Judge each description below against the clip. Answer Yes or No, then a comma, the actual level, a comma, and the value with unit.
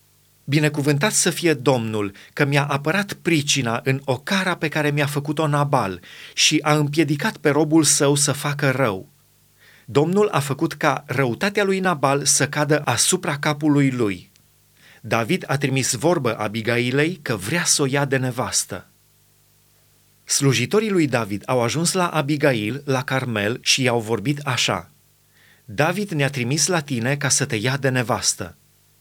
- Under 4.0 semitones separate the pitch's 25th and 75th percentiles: Yes, average, 3.1 semitones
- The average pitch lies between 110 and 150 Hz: Yes, medium, 140 Hz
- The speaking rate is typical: Yes, average, 150 wpm